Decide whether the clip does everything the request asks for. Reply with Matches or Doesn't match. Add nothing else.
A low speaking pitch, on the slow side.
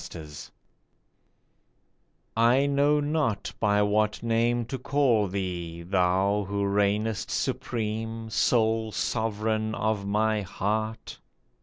Matches